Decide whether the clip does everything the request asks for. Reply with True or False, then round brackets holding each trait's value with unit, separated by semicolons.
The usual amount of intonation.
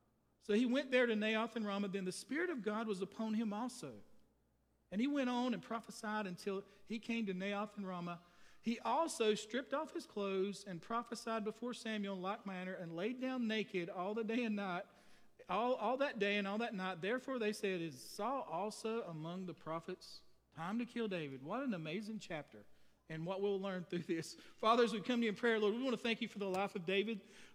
True (3.7 semitones)